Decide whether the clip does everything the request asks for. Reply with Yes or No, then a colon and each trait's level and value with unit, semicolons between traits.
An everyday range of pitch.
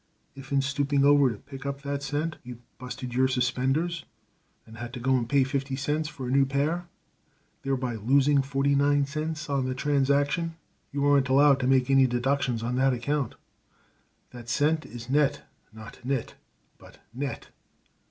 No: narrow, 1.9 semitones